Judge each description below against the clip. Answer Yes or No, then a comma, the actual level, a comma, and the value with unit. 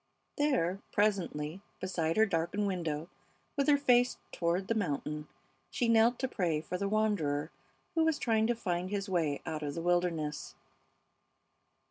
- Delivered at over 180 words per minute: No, average, 150 wpm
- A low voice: No, medium, 185 Hz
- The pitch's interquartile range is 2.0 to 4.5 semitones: No, average, 5.3 semitones